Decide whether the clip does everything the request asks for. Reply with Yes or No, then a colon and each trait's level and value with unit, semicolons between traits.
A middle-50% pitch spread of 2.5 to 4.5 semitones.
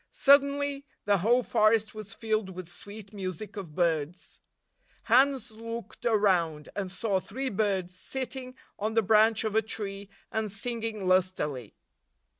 Yes: average, 3.5 semitones